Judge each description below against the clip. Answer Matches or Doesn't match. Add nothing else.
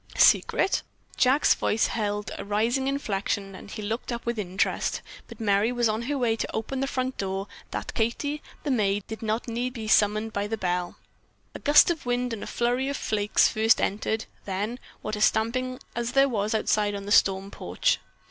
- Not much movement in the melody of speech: Doesn't match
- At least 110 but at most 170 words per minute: Doesn't match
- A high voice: Matches